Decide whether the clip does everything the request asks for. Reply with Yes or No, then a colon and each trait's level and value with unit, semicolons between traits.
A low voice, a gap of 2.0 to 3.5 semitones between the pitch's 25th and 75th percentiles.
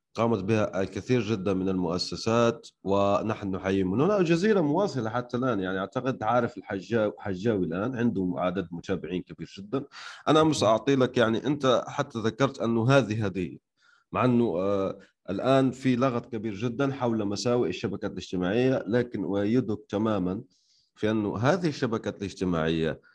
No: low, 110 Hz; average, 4.4 semitones